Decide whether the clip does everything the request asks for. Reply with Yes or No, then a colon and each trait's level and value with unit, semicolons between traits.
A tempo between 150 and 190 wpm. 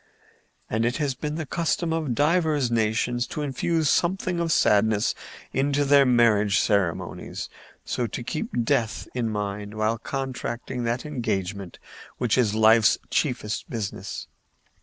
No: slow, 135 wpm